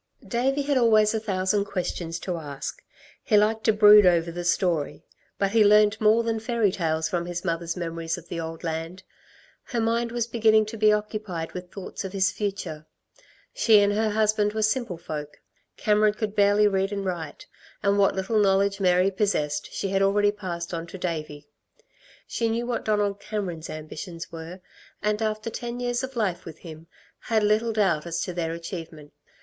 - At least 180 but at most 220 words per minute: Yes, average, 185 wpm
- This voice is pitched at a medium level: No, high, 200 Hz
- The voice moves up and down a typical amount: Yes, average, 4.0 semitones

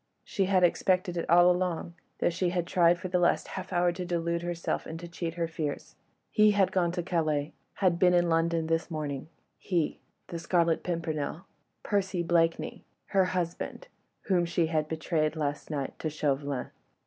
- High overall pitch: No, medium, 170 Hz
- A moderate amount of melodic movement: No, narrow, 1.9 semitones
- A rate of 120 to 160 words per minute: No, average, 175 wpm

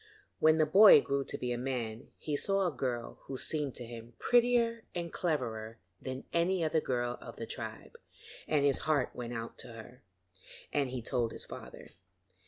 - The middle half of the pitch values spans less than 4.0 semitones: No, average, 4.8 semitones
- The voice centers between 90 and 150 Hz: Yes, low, 135 Hz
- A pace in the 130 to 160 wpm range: No, average, 185 wpm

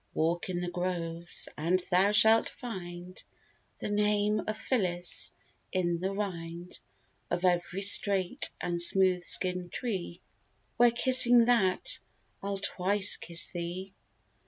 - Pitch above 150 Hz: Yes, medium, 185 Hz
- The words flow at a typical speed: No, slow, 120 wpm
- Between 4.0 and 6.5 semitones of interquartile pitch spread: No, average, 2.9 semitones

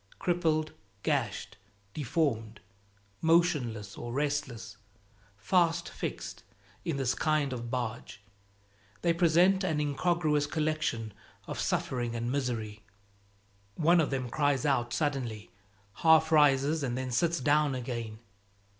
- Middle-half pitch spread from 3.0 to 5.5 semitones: Yes, average, 4.8 semitones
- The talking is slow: Yes, slow, 110 wpm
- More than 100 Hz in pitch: Yes, medium, 140 Hz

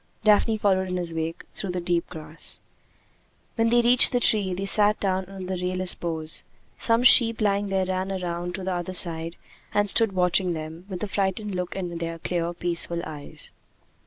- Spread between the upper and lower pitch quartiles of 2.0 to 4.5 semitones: Yes, average, 2.7 semitones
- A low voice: No, medium, 185 Hz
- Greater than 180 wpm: Yes, average, 190 wpm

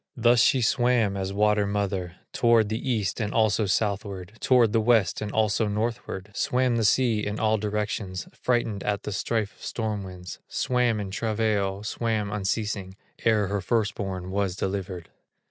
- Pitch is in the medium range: No, low, 105 Hz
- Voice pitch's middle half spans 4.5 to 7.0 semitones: No, narrow, 2.4 semitones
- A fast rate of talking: No, average, 165 wpm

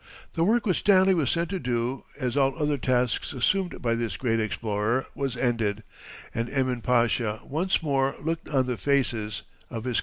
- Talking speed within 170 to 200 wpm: Yes, average, 185 wpm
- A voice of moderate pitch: No, low, 130 Hz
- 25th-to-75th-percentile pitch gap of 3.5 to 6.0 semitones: Yes, average, 4.2 semitones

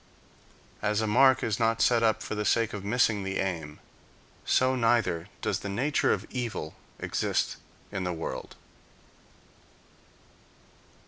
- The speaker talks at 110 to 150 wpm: Yes, slow, 135 wpm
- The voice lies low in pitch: Yes, low, 110 Hz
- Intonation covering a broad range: No, average, 3.7 semitones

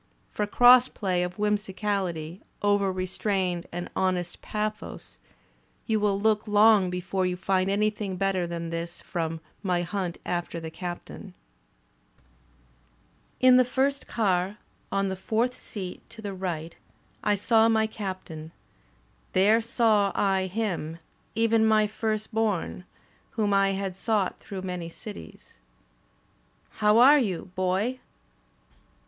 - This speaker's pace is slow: Yes, slow, 125 wpm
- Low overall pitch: No, high, 195 Hz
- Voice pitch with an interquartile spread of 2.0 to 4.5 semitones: Yes, average, 3.1 semitones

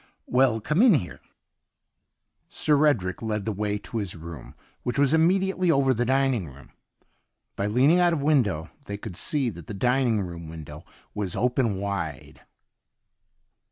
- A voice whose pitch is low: Yes, low, 115 Hz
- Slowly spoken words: No, average, 160 wpm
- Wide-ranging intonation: Yes, wide, 6.5 semitones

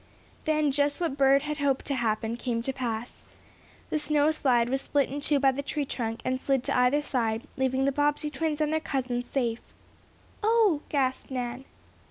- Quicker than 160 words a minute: Yes, average, 190 wpm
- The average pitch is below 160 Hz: No, very high, 270 Hz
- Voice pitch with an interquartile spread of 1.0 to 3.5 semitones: Yes, average, 2.9 semitones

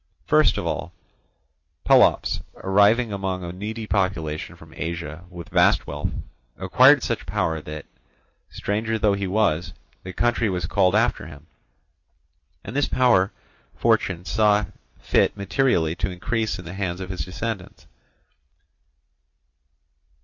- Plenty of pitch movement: No, average, 3.8 semitones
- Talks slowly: Yes, slow, 130 wpm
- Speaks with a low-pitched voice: Yes, very low, 95 Hz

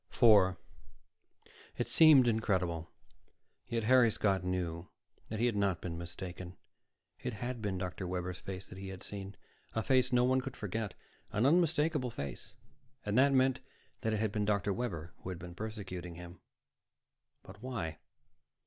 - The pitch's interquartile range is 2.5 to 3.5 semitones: No, average, 5.1 semitones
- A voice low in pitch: Yes, low, 100 Hz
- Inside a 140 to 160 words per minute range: Yes, average, 150 wpm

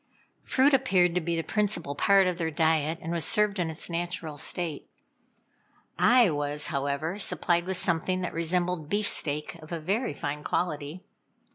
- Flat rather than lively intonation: No, average, 3.1 semitones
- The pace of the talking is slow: No, average, 160 wpm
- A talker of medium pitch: Yes, medium, 170 Hz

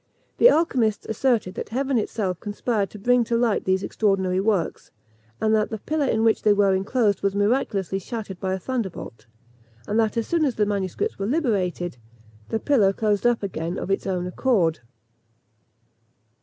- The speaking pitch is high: Yes, high, 210 Hz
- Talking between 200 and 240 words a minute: No, average, 170 wpm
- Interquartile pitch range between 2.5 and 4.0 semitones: Yes, average, 3.7 semitones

